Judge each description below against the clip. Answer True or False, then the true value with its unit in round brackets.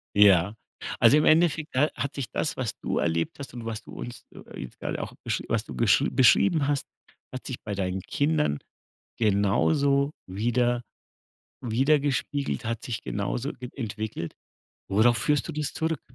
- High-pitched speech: False (125 Hz)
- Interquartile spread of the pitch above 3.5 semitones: True (5.3 semitones)